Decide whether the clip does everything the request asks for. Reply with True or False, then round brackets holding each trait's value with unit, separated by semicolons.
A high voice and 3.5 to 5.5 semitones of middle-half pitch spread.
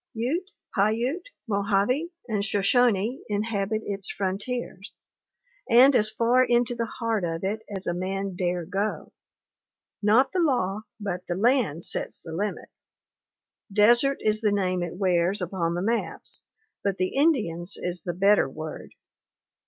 True (205 Hz; 4.2 semitones)